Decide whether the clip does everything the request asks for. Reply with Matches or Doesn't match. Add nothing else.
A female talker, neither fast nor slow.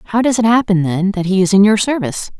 Doesn't match